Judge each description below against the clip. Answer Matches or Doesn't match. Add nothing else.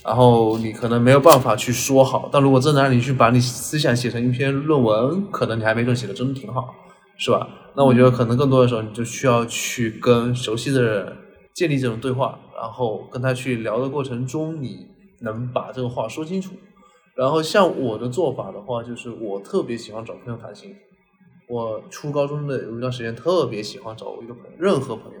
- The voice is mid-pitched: Doesn't match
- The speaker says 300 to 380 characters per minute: Matches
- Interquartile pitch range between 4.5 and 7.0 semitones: Doesn't match